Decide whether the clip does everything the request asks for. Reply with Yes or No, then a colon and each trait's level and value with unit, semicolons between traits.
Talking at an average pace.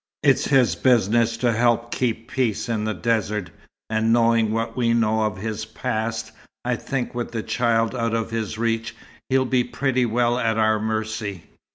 Yes: average, 175 wpm